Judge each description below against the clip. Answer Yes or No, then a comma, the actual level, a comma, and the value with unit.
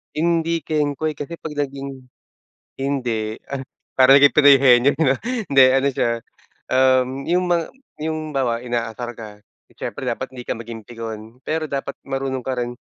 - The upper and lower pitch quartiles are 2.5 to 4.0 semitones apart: Yes, average, 3.5 semitones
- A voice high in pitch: No, low, 135 Hz